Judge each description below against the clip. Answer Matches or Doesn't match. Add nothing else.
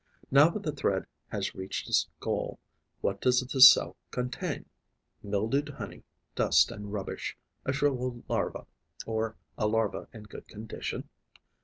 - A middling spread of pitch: Matches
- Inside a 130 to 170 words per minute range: Matches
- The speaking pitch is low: Matches